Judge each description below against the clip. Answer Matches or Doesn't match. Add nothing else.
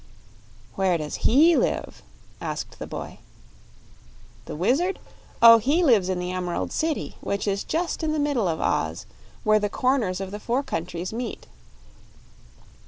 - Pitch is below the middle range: Doesn't match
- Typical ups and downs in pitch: Doesn't match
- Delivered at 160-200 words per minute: Doesn't match